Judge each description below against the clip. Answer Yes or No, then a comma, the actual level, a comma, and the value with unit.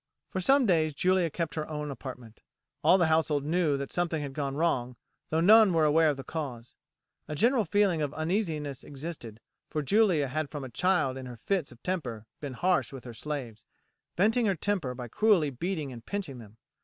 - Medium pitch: Yes, medium, 155 Hz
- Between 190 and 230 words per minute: Yes, average, 195 wpm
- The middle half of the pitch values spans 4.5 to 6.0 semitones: Yes, average, 5.1 semitones